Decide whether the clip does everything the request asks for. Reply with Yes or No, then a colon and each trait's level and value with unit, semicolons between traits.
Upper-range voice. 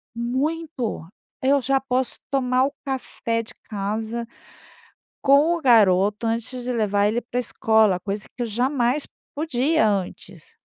Yes: high, 240 Hz